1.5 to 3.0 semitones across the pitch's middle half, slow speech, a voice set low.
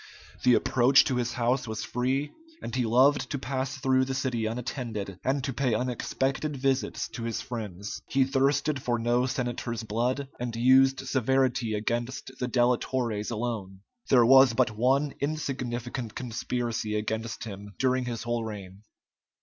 No: narrow, 2.4 semitones; average, 150 wpm; low, 125 Hz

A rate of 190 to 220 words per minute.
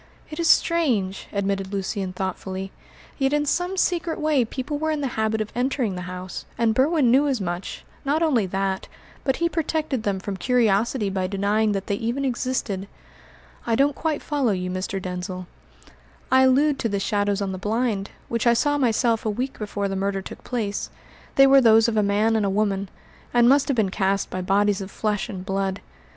Yes: average, 195 wpm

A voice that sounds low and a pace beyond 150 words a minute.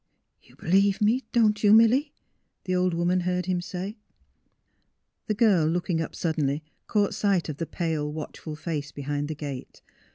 No: medium, 180 Hz; average, 170 wpm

